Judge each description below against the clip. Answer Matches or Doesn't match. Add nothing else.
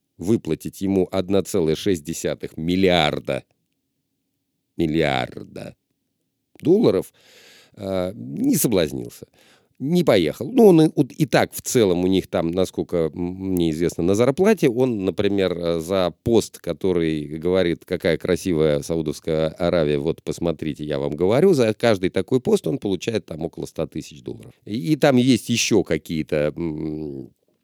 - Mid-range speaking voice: Doesn't match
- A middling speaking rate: Matches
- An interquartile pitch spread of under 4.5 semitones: Doesn't match